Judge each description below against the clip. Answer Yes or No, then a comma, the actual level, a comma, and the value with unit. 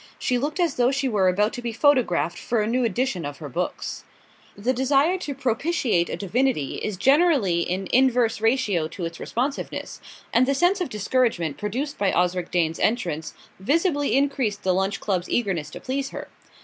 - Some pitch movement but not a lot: No, wide, 6.6 semitones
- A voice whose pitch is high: Yes, high, 230 Hz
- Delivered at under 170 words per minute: No, average, 180 wpm